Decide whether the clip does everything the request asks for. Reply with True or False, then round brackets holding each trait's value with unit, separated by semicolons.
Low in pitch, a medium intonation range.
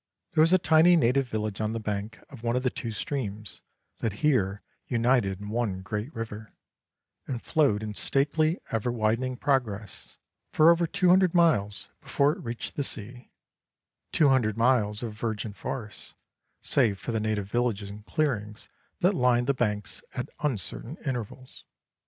True (115 Hz; 4.6 semitones)